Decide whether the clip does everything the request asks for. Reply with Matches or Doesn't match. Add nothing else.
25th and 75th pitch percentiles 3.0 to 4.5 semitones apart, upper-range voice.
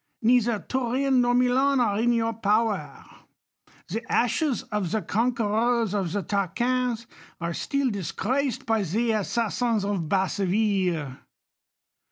Matches